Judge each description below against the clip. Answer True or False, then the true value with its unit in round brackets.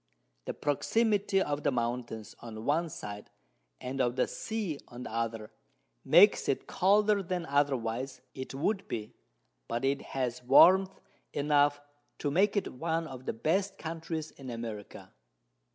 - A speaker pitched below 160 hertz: True (140 Hz)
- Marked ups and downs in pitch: True (6.3 semitones)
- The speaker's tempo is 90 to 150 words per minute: True (145 wpm)